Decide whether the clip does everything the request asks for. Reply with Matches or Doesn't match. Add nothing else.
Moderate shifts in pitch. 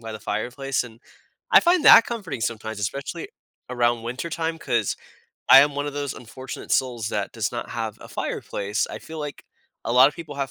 Matches